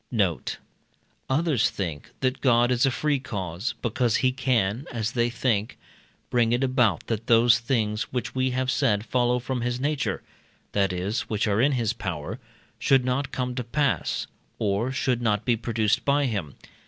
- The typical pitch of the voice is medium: No, low, 120 Hz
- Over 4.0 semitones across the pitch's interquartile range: No, average, 3.3 semitones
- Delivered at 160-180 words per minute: Yes, average, 170 wpm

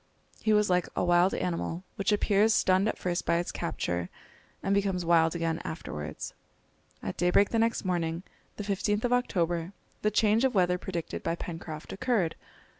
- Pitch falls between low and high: Yes, medium, 180 Hz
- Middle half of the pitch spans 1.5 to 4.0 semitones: Yes, average, 3.6 semitones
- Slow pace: No, average, 170 wpm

